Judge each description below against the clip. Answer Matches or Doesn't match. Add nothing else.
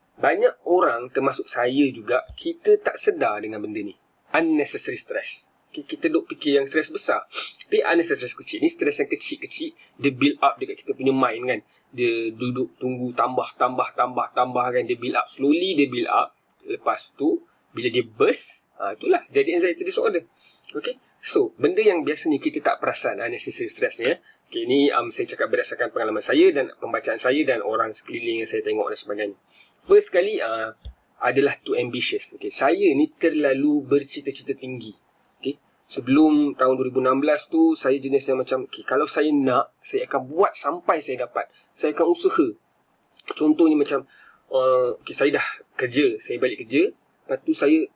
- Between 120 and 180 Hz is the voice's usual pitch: Doesn't match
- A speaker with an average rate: Doesn't match